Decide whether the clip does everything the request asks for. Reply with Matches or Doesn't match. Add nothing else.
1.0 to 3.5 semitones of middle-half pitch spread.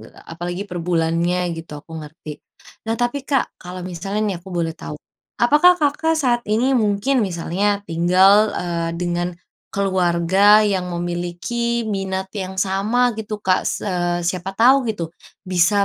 Doesn't match